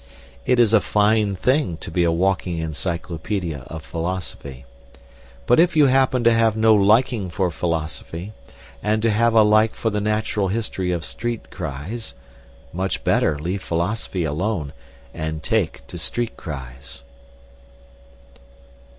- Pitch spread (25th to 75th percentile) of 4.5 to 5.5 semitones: Yes, average, 5.1 semitones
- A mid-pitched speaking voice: No, very low, 95 Hz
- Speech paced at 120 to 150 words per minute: Yes, average, 140 wpm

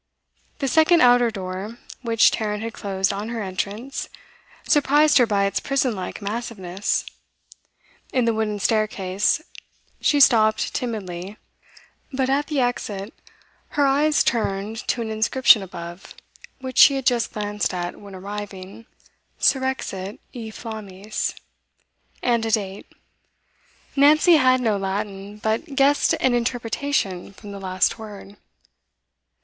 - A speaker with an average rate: No, slow, 125 wpm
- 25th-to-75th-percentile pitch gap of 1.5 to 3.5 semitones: No, average, 4.4 semitones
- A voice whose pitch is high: Yes, high, 220 Hz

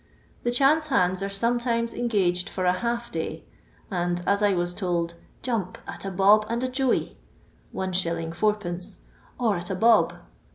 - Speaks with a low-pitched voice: No, high, 200 Hz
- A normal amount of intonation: Yes, average, 4.8 semitones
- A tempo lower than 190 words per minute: Yes, average, 160 wpm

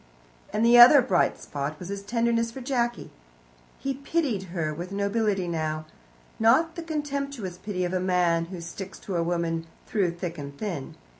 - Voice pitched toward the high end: Yes, high, 195 Hz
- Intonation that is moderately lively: No, wide, 5.7 semitones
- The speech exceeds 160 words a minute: Yes, average, 170 wpm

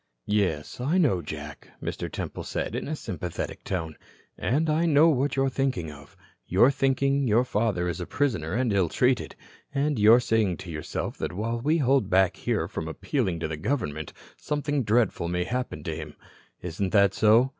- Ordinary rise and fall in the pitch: No, wide, 7.5 semitones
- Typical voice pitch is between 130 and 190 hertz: No, low, 110 Hz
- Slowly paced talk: No, average, 180 wpm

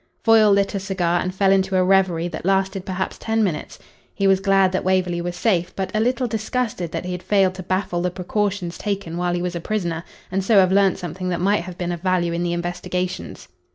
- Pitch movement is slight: Yes, narrow, 1.9 semitones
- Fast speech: Yes, fast, 230 wpm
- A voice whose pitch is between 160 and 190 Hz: Yes, medium, 185 Hz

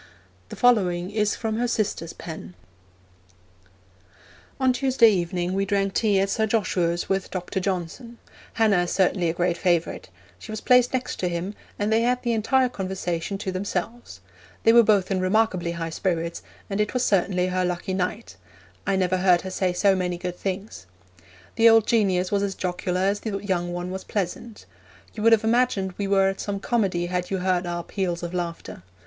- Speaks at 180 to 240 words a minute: Yes, average, 185 wpm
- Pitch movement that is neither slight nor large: Yes, average, 3.3 semitones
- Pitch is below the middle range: No, high, 190 Hz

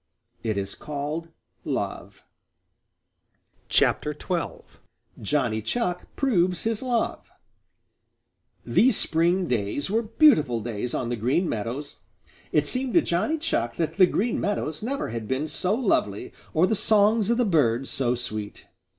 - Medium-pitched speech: Yes, medium, 165 Hz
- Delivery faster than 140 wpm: No, slow, 135 wpm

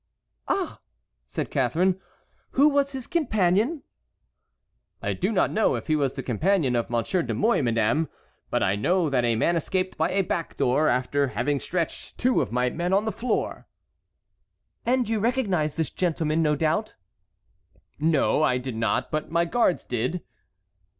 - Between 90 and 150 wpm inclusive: No, average, 165 wpm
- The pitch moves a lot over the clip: Yes, wide, 7.4 semitones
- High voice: No, medium, 165 Hz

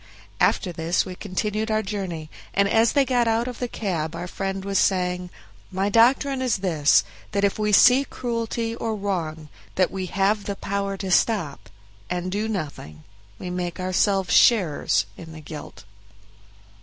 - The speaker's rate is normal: Yes, average, 165 wpm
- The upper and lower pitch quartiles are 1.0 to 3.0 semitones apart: No, average, 3.7 semitones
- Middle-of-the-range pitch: No, high, 195 Hz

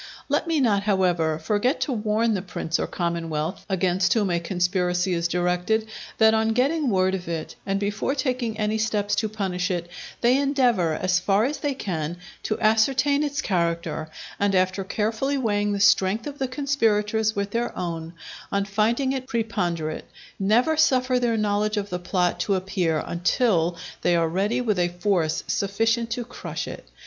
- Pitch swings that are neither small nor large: Yes, average, 4.5 semitones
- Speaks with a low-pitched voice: No, high, 205 Hz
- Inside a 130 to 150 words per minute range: No, average, 175 wpm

